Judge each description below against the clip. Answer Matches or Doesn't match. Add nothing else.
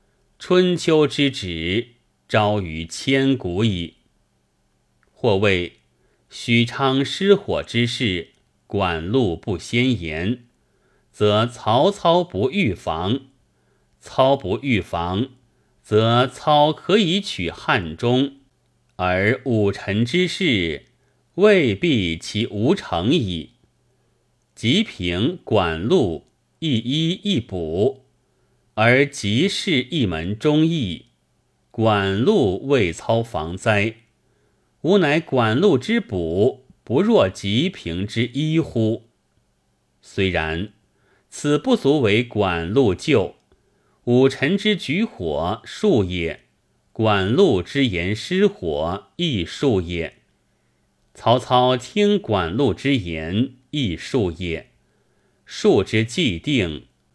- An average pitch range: Doesn't match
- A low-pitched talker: Matches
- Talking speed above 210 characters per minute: Doesn't match